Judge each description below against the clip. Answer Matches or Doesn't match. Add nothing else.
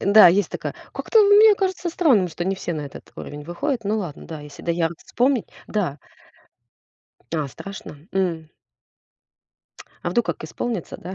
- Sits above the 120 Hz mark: Matches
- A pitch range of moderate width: Doesn't match